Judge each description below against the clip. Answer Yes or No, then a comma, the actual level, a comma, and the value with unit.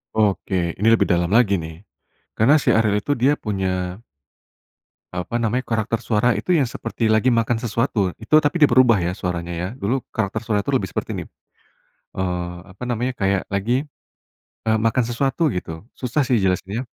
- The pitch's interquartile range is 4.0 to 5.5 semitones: Yes, average, 4.3 semitones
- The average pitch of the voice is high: No, low, 110 Hz